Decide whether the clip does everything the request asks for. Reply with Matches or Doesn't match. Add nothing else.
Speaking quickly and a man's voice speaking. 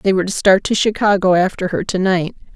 Doesn't match